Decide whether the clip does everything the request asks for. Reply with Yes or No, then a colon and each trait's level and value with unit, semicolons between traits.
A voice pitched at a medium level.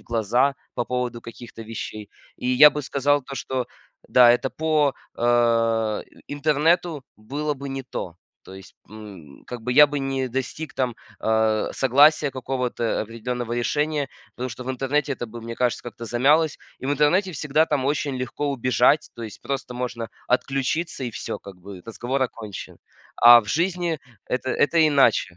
No: low, 130 Hz